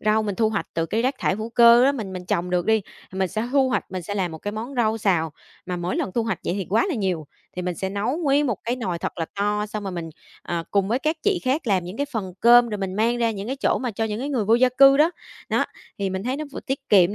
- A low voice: No, high, 215 Hz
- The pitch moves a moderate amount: Yes, average, 4.4 semitones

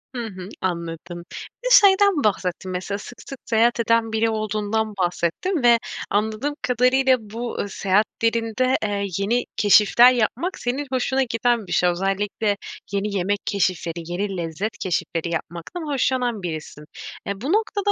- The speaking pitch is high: Yes, high, 215 Hz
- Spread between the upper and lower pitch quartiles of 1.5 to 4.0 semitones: No, average, 4.5 semitones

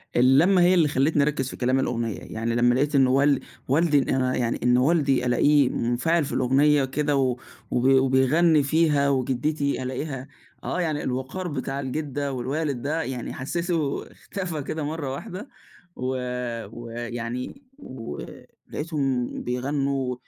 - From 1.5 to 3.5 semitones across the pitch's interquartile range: Yes, average, 2.9 semitones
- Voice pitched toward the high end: No, low, 135 Hz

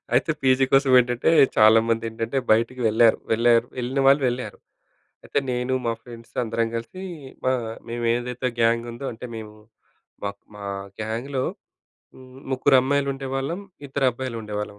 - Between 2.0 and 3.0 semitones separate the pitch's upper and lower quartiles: Yes, narrow, 2.5 semitones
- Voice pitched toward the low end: Yes, low, 120 Hz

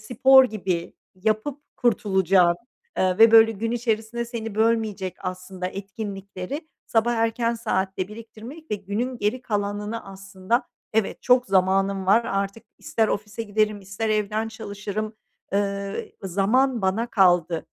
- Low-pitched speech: No, high, 210 Hz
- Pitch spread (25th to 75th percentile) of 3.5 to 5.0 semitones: No, average, 2.8 semitones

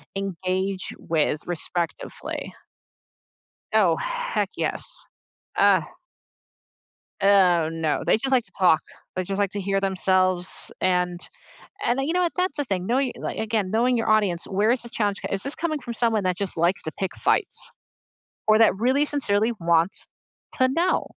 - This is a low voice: No, high, 200 Hz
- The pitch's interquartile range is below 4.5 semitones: No, average, 4.9 semitones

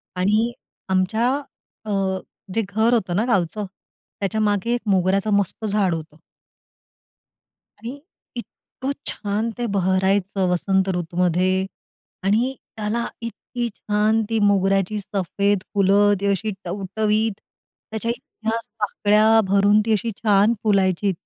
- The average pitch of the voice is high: Yes, high, 205 Hz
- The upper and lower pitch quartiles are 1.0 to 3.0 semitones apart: Yes, narrow, 2.5 semitones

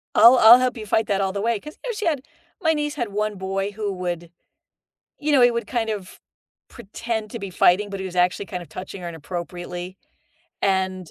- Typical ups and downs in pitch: Yes, average, 4.1 semitones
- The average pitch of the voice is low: No, high, 200 Hz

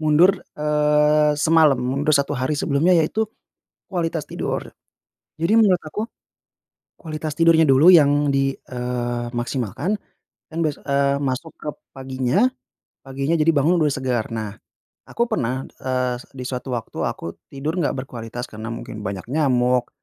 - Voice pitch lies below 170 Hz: Yes, medium, 140 Hz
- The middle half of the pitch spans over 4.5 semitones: No, average, 3.8 semitones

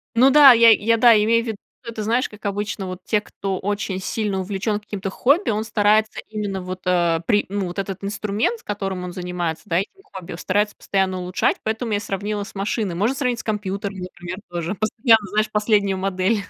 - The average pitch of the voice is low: No, high, 205 Hz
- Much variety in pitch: No, narrow, 2.6 semitones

